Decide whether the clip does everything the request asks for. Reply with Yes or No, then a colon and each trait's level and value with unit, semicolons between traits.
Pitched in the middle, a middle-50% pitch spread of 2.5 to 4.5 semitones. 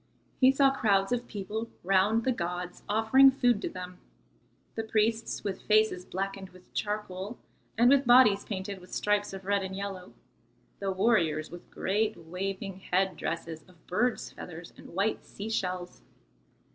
No: high, 200 Hz; average, 3.3 semitones